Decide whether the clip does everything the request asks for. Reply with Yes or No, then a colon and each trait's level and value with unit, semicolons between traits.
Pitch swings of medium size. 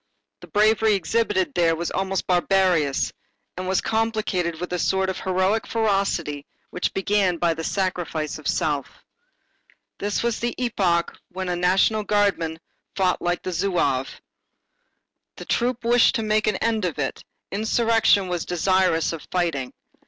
Yes: average, 3.6 semitones